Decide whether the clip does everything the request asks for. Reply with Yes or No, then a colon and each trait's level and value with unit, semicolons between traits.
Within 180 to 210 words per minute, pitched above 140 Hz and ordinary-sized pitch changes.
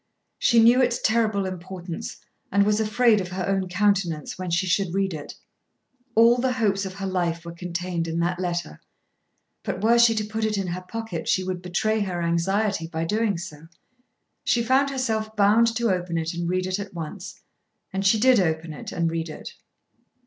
Yes: average, 190 wpm; high, 190 Hz; average, 4.0 semitones